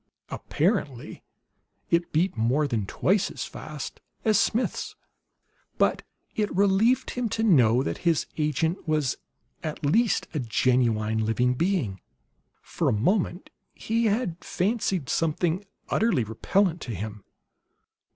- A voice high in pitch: No, medium, 160 Hz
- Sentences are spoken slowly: Yes, slow, 120 wpm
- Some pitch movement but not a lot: No, wide, 8.3 semitones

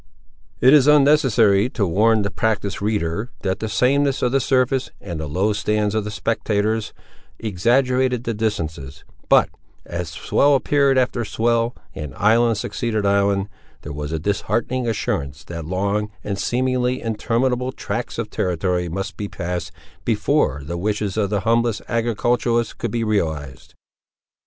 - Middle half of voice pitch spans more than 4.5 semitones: No, average, 3.8 semitones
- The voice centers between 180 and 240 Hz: No, low, 105 Hz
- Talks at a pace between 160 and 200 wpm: No, average, 145 wpm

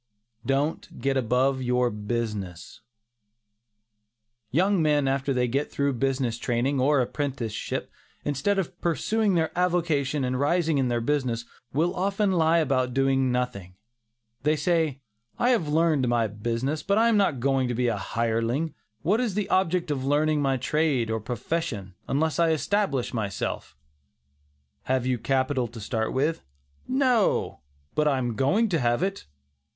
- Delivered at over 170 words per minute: No, average, 155 wpm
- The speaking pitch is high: No, low, 135 Hz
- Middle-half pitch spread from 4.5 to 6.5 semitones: Yes, average, 4.9 semitones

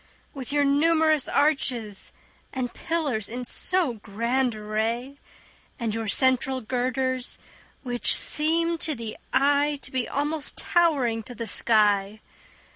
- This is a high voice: Yes, very high, 260 Hz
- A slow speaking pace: Yes, slow, 120 wpm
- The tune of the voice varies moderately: Yes, average, 4.4 semitones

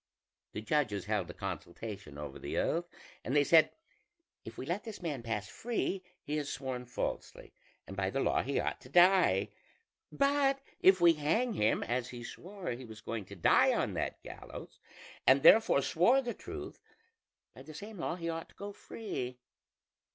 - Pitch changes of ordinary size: No, wide, 8.5 semitones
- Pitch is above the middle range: No, medium, 145 Hz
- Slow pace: No, average, 180 wpm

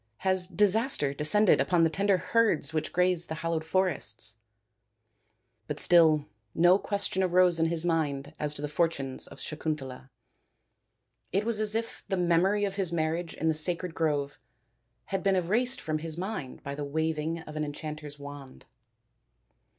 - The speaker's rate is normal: Yes, average, 165 wpm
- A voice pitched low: No, medium, 165 Hz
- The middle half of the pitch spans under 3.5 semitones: No, average, 3.9 semitones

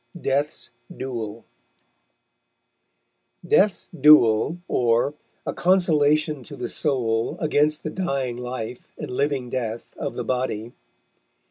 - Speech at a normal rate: No, slow, 105 wpm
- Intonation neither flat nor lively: Yes, average, 4.2 semitones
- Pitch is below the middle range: Yes, low, 130 Hz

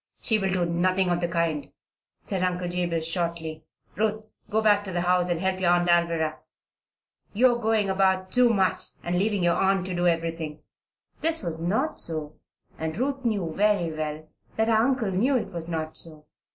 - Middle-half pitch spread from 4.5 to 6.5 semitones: No, average, 3.7 semitones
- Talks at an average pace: Yes, average, 190 wpm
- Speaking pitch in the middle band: Yes, medium, 180 Hz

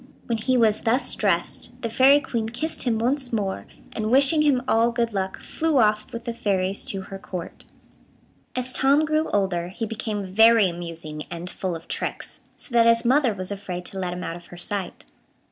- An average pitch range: Yes, average, 4.6 semitones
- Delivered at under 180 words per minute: No, average, 195 wpm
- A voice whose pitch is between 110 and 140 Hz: No, high, 220 Hz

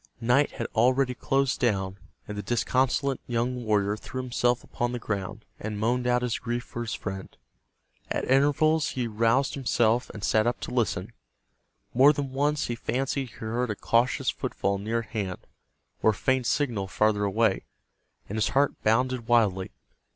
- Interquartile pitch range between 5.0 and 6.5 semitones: No, average, 3.0 semitones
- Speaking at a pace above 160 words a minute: Yes, average, 170 wpm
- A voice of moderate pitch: No, low, 120 Hz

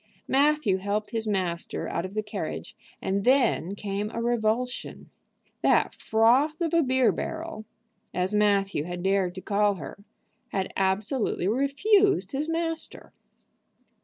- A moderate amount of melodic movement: No, wide, 5.8 semitones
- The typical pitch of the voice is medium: No, high, 215 Hz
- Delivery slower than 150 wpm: Yes, slow, 135 wpm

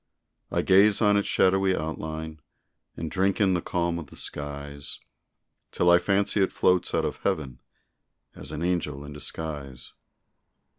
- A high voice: No, very low, 85 Hz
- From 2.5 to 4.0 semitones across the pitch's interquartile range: No, average, 4.5 semitones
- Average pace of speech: Yes, average, 150 wpm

